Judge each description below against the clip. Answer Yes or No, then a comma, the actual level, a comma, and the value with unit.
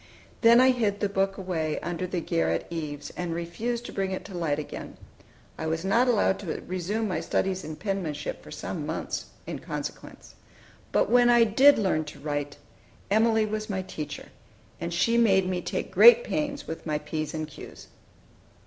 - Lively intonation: Yes, wide, 5.7 semitones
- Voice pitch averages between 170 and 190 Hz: Yes, medium, 185 Hz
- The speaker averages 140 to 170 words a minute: No, average, 180 wpm